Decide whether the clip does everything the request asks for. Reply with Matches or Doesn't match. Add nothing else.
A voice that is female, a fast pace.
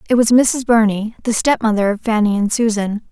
Doesn't match